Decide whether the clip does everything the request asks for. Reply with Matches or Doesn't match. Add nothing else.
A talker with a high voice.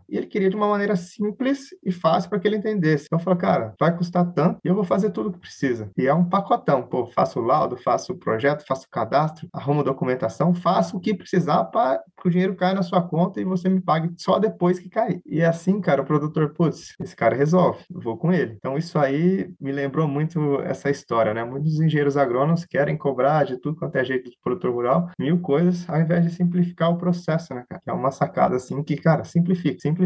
Doesn't match